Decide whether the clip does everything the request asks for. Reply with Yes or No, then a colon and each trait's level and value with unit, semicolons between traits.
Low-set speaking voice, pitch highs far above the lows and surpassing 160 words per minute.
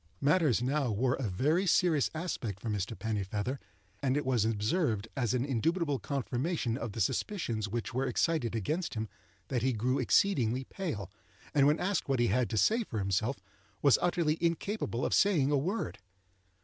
Yes: low, 130 Hz; wide, 6.0 semitones; average, 175 wpm